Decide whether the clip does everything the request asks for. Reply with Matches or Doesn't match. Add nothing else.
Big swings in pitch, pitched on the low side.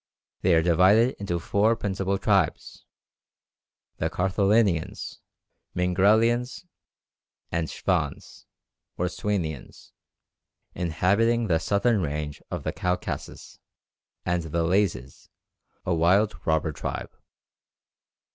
Doesn't match